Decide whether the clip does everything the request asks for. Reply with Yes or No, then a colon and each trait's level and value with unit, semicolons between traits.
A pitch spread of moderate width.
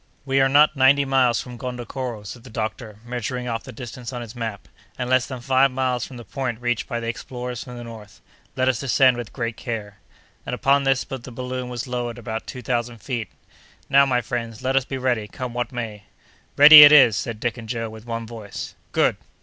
No: narrow, 2.1 semitones